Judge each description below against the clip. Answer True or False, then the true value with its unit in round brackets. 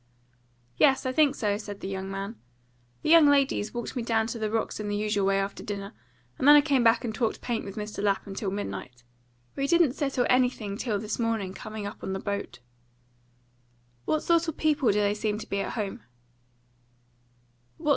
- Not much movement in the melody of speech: False (4.2 semitones)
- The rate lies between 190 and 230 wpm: True (195 wpm)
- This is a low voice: False (215 Hz)